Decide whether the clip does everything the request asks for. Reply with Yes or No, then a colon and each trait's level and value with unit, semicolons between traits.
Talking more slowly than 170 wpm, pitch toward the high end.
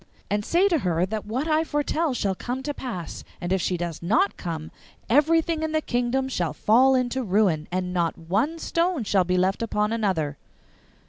No: average, 190 wpm; high, 220 Hz